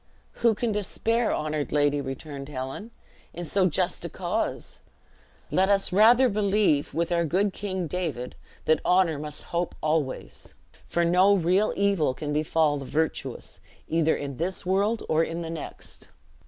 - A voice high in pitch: No, medium, 170 Hz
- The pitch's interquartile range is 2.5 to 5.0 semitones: Yes, average, 4.7 semitones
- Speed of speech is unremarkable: Yes, average, 155 wpm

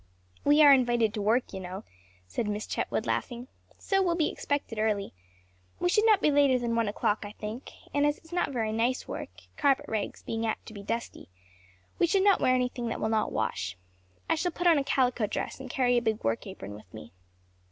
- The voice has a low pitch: No, high, 240 Hz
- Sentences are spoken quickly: Yes, fast, 220 wpm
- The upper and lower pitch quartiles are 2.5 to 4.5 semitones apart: No, average, 5.1 semitones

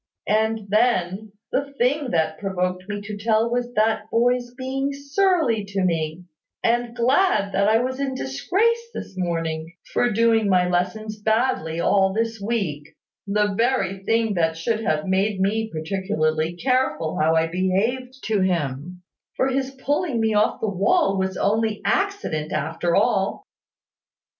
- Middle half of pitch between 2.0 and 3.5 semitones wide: No, average, 5.2 semitones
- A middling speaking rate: Yes, average, 150 wpm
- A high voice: Yes, high, 210 Hz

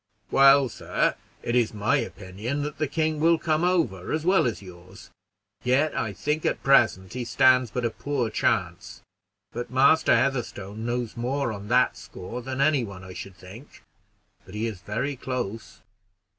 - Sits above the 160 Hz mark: No, low, 125 Hz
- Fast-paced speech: No, average, 170 wpm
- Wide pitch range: No, average, 5.0 semitones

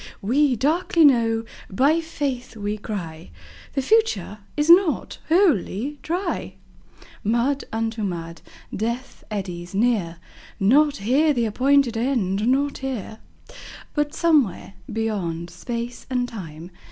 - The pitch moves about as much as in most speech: No, wide, 5.9 semitones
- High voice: Yes, high, 235 Hz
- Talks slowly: Yes, slow, 115 wpm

